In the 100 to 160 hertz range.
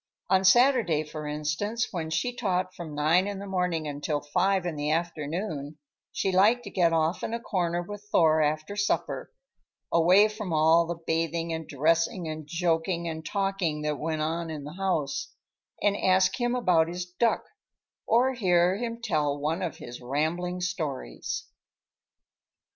No: medium, 170 Hz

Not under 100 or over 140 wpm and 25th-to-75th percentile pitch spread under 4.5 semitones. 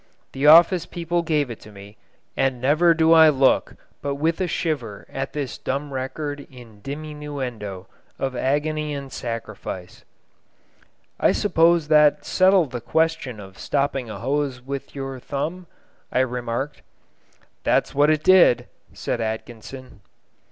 Yes: slow, 135 wpm; average, 3.9 semitones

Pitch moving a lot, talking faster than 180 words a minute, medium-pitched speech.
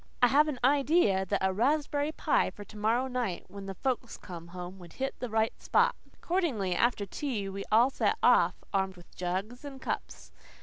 No: wide, 5.9 semitones; average, 190 wpm; high, 220 Hz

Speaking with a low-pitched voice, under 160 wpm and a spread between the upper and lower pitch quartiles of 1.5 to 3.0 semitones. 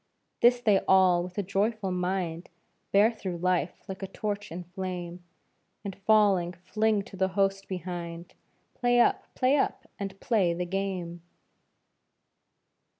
No: high, 190 Hz; average, 140 wpm; narrow, 2.4 semitones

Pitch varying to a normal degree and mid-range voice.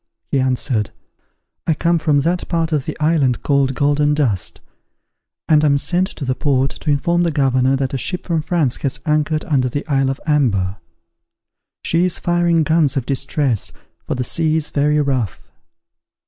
Yes: average, 3.2 semitones; medium, 145 Hz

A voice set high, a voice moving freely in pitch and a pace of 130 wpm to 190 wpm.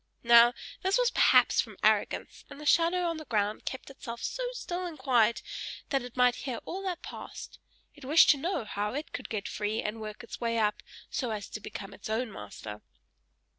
No: high, 245 Hz; wide, 6.2 semitones; fast, 205 wpm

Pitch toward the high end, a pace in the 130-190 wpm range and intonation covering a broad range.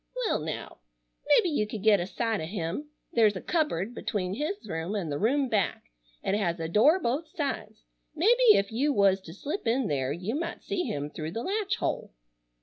No: high, 215 Hz; average, 200 wpm; wide, 8.5 semitones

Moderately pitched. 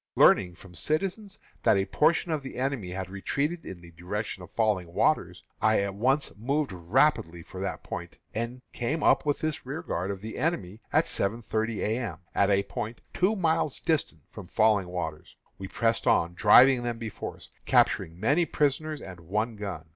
No: low, 110 Hz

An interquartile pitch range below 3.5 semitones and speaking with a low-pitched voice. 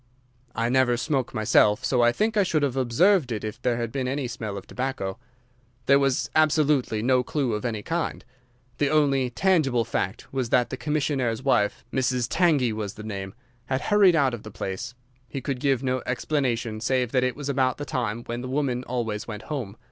Yes: average, 3.1 semitones; low, 125 Hz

